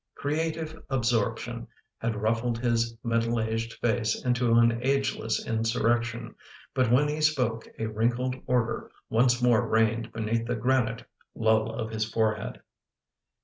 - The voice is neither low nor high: No, low, 115 Hz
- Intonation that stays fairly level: Yes, narrow, 1.7 semitones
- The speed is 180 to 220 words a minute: No, average, 140 wpm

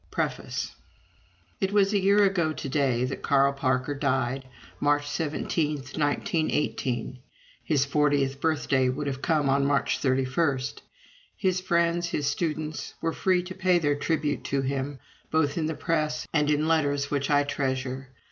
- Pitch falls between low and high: Yes, medium, 145 Hz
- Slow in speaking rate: No, average, 155 wpm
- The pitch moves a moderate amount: Yes, average, 3.0 semitones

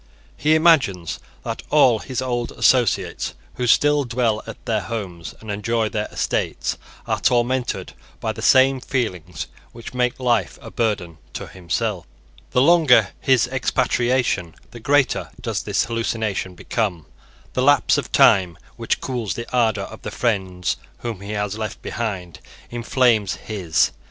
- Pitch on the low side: Yes, low, 115 Hz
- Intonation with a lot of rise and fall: No, average, 4.1 semitones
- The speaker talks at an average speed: Yes, average, 145 wpm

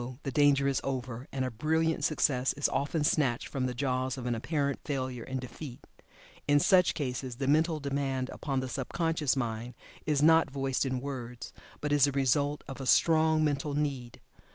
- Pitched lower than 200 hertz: Yes, medium, 140 Hz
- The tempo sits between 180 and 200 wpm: Yes, average, 185 wpm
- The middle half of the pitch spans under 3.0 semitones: Yes, narrow, 2.5 semitones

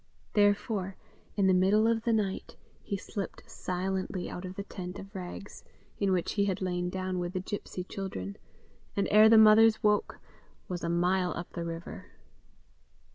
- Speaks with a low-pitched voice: No, high, 190 Hz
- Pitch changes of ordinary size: No, narrow, 2.3 semitones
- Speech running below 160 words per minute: No, average, 170 wpm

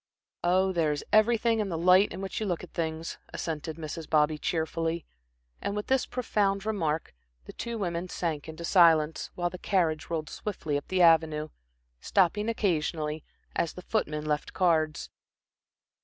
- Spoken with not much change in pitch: No, average, 3.6 semitones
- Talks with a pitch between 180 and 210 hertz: No, medium, 170 Hz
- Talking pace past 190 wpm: No, average, 160 wpm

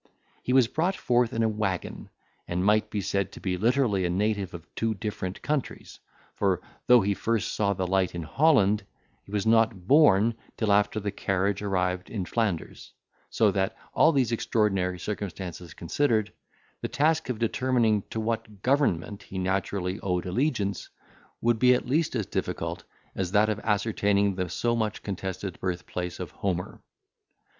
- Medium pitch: No, low, 105 Hz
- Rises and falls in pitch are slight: No, average, 3.5 semitones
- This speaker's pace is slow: No, average, 165 wpm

